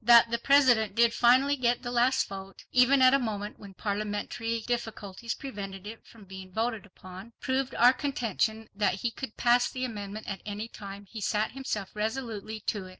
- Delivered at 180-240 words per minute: Yes, average, 185 wpm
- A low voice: No, high, 225 Hz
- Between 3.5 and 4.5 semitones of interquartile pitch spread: No, average, 3.1 semitones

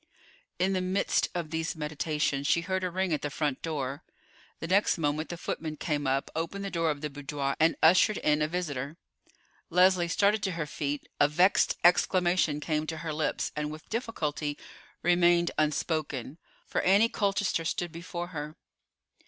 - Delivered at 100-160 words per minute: No, average, 170 wpm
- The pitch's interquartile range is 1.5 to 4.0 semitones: Yes, average, 3.2 semitones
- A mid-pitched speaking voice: Yes, medium, 160 Hz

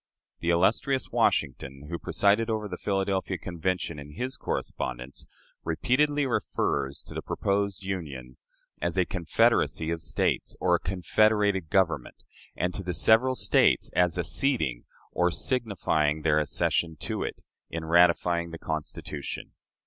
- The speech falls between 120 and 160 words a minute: Yes, slow, 135 wpm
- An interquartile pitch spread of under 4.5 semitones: Yes, average, 4.1 semitones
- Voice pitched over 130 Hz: No, very low, 90 Hz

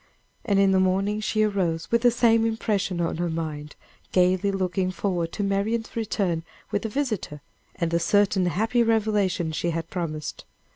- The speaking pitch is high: Yes, high, 195 Hz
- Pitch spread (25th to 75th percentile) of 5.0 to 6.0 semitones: No, average, 4.0 semitones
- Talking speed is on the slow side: No, average, 165 wpm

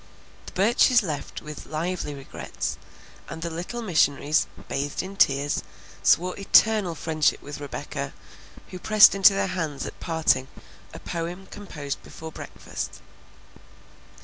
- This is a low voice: No, medium, 165 Hz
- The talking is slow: Yes, slow, 125 wpm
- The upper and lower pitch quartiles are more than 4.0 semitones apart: Yes, average, 4.7 semitones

